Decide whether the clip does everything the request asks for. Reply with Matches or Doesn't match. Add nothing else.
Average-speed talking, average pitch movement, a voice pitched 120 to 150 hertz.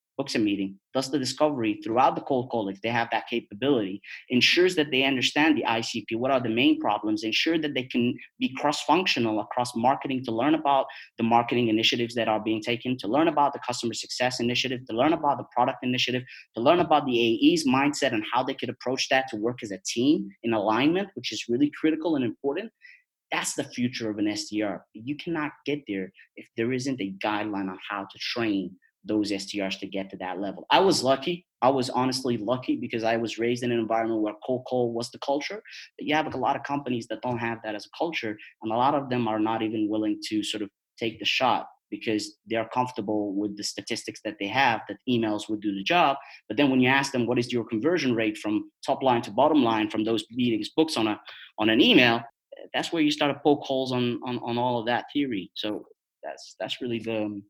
Doesn't match